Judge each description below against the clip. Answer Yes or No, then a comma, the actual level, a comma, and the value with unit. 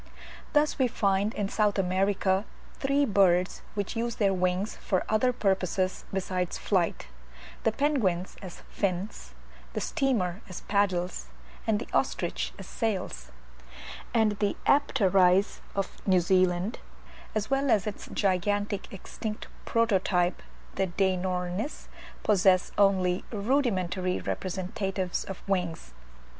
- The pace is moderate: No, slow, 115 wpm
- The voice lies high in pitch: Yes, high, 195 Hz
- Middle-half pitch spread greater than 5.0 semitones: No, average, 2.7 semitones